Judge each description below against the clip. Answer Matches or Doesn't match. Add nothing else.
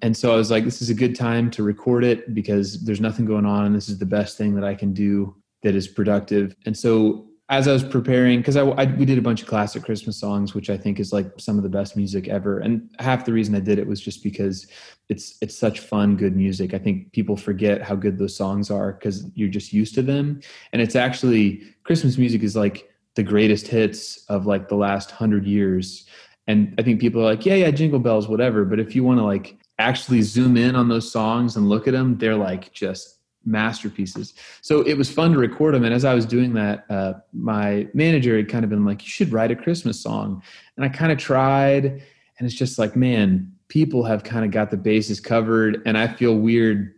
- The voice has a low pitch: Matches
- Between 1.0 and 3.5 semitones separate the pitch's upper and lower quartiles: Matches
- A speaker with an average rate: Doesn't match